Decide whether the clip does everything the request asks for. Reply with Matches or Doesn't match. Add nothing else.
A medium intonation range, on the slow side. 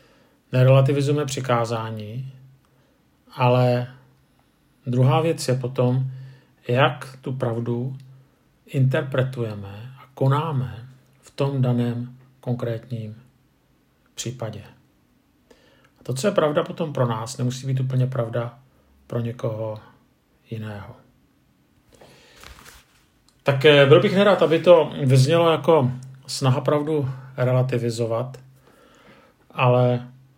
Doesn't match